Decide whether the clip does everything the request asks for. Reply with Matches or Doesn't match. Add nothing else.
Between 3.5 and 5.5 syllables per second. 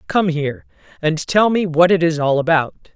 Matches